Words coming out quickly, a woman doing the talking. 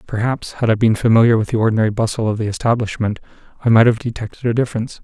No: fast, 215 wpm; male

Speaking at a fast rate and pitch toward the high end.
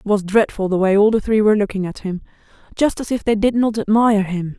Yes: fast, 260 wpm; high, 210 Hz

